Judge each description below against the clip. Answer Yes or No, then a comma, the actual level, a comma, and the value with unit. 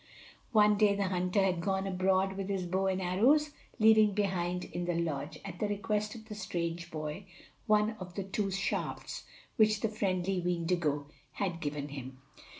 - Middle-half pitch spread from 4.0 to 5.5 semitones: No, average, 3.0 semitones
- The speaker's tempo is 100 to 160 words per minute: No, average, 175 wpm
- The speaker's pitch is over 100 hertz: Yes, high, 190 Hz